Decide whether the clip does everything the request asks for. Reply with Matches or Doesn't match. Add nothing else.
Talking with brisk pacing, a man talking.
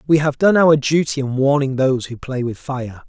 Matches